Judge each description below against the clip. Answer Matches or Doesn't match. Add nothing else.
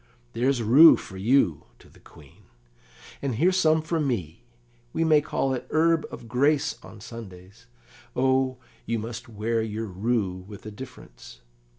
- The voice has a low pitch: Matches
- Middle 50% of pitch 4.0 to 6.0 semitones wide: Matches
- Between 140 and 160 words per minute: Matches